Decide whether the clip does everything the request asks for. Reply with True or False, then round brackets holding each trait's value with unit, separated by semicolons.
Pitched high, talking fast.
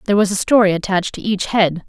True (195 Hz; 255 wpm)